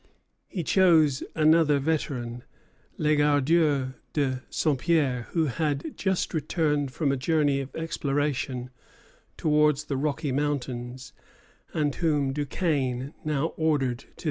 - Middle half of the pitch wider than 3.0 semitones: No, average, 2.7 semitones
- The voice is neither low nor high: Yes, medium, 145 Hz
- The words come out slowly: Yes, slow, 120 wpm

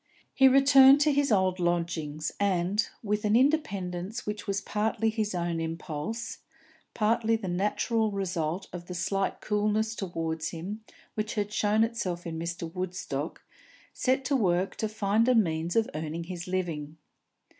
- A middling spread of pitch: Yes, average, 4.2 semitones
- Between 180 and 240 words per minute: No, average, 150 wpm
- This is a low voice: No, high, 195 Hz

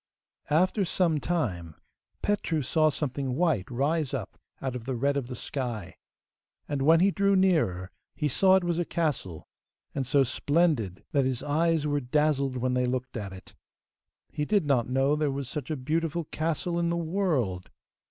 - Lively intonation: No, average, 4.7 semitones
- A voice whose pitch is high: No, medium, 145 Hz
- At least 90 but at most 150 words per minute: No, average, 175 wpm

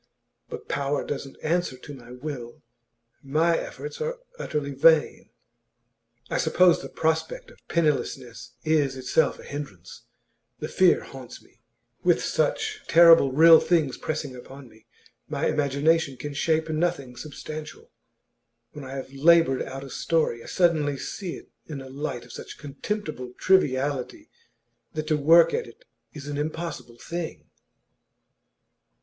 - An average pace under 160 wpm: Yes, average, 140 wpm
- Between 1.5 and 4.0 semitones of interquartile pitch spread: Yes, average, 3.4 semitones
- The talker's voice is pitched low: No, medium, 145 Hz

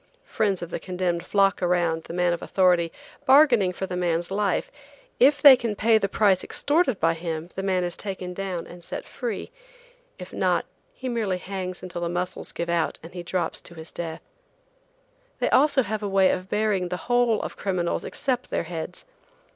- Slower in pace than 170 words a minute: No, average, 185 wpm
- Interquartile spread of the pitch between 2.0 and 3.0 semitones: No, average, 3.4 semitones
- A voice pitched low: No, medium, 185 Hz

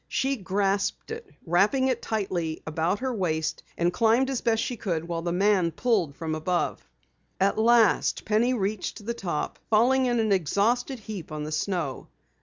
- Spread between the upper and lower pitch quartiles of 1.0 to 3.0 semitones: No, wide, 5.4 semitones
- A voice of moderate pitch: No, high, 200 Hz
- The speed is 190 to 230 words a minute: No, average, 170 wpm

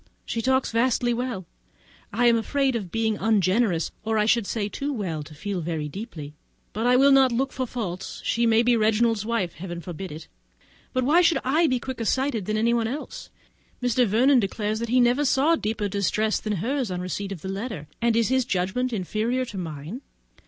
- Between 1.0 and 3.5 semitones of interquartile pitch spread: No, average, 4.4 semitones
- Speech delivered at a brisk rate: Yes, fast, 210 wpm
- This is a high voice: Yes, high, 225 Hz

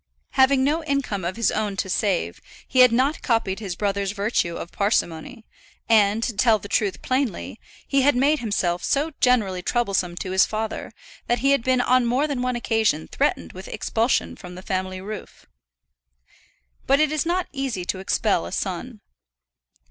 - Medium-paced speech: Yes, average, 170 wpm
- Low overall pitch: No, high, 225 Hz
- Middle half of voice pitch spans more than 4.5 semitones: Yes, average, 5.1 semitones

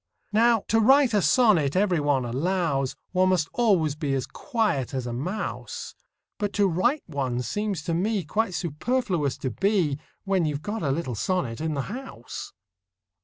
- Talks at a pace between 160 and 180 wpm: Yes, average, 170 wpm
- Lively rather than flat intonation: Yes, wide, 6.8 semitones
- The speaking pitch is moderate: Yes, medium, 175 Hz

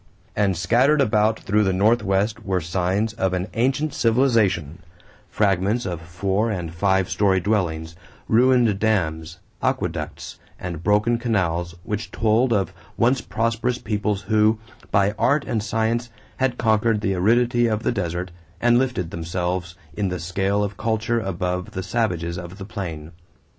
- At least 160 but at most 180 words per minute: No, average, 145 wpm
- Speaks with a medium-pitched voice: No, low, 100 Hz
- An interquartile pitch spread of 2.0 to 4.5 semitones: Yes, average, 4.0 semitones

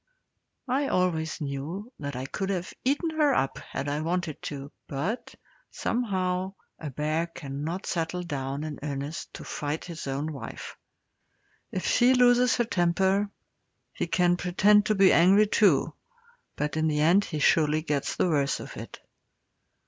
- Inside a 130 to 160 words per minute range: Yes, average, 155 wpm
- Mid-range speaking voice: Yes, medium, 170 Hz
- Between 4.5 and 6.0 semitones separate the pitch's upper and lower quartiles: Yes, average, 4.8 semitones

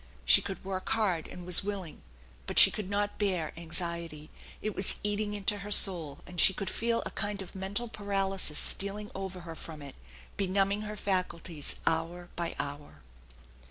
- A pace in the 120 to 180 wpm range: Yes, average, 170 wpm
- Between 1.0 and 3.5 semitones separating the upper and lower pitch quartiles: Yes, average, 3.2 semitones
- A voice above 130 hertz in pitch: Yes, high, 190 Hz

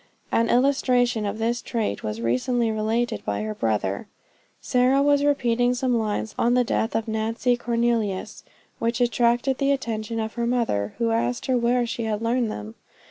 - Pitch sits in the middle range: No, high, 235 Hz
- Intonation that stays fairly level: Yes, narrow, 2.1 semitones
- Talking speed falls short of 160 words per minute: No, average, 170 wpm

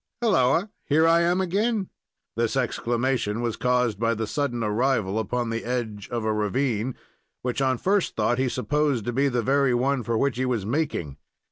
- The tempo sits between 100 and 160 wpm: No, average, 180 wpm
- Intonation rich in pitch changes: No, average, 3.6 semitones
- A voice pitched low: Yes, low, 125 Hz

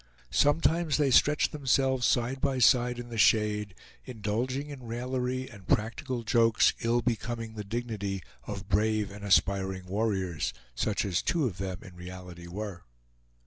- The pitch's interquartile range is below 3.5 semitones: No, average, 4.2 semitones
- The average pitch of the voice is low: Yes, low, 110 Hz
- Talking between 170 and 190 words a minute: No, average, 145 wpm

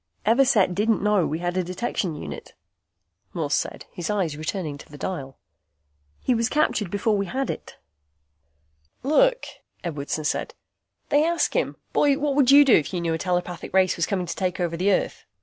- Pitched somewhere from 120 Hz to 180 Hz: No, high, 190 Hz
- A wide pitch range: Yes, wide, 6.5 semitones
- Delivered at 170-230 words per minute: Yes, average, 180 wpm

